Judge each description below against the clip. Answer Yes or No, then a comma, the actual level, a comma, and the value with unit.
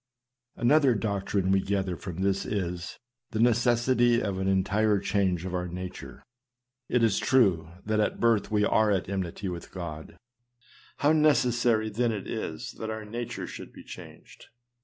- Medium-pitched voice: No, low, 105 Hz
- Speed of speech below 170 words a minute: Yes, average, 160 wpm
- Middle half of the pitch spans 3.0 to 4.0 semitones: Yes, average, 3.7 semitones